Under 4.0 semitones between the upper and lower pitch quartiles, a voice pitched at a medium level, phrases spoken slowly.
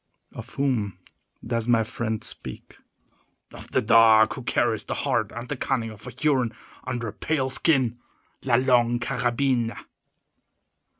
No: narrow, 2.4 semitones; low, 120 Hz; slow, 130 wpm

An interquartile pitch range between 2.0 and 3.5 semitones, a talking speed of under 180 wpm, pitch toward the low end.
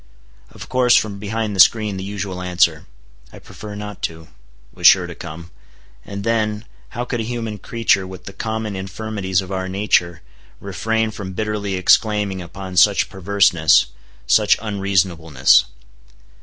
Yes: average, 2.9 semitones; average, 140 wpm; low, 100 Hz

